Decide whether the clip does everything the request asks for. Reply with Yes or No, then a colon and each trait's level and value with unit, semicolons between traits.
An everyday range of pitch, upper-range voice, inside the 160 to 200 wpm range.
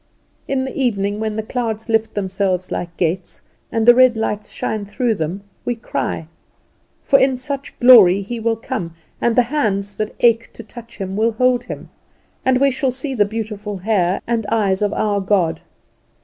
Yes: average, 3.5 semitones; high, 220 Hz; average, 180 wpm